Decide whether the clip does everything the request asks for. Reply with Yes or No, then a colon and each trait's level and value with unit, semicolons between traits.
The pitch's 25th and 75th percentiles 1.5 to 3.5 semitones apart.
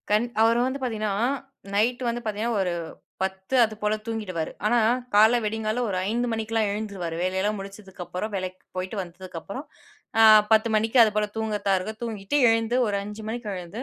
Yes: average, 2.7 semitones